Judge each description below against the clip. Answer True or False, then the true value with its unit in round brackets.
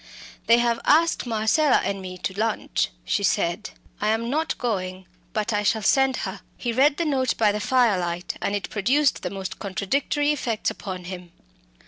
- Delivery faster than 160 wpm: True (175 wpm)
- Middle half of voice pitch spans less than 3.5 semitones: False (5.1 semitones)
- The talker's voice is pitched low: False (220 Hz)